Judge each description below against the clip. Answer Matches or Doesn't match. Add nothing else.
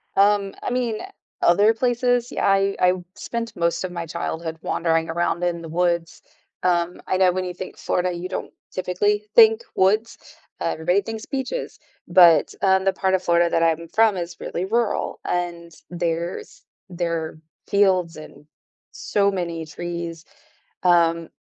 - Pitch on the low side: Doesn't match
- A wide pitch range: Doesn't match